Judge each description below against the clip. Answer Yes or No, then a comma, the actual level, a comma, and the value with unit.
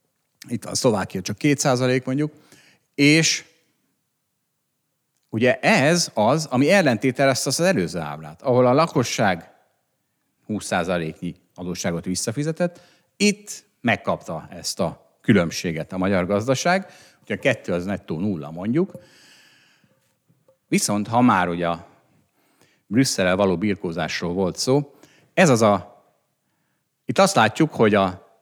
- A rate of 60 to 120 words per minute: Yes, average, 110 wpm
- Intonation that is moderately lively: No, wide, 8.5 semitones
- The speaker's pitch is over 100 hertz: Yes, low, 125 Hz